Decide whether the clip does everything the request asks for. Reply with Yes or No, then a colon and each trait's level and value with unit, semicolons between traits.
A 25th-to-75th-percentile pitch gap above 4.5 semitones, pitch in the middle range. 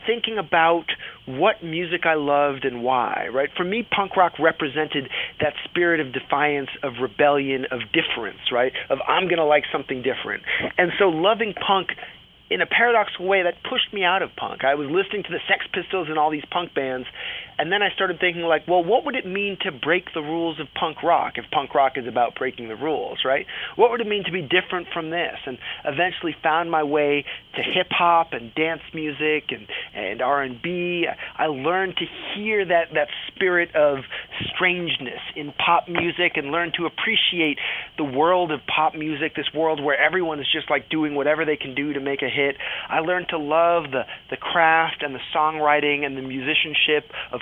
No: average, 3.4 semitones; medium, 160 Hz